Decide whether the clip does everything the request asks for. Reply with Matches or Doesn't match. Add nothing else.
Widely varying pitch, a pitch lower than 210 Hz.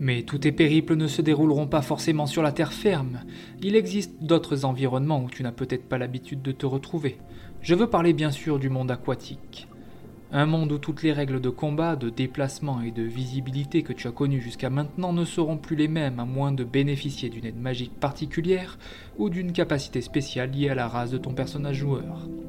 Doesn't match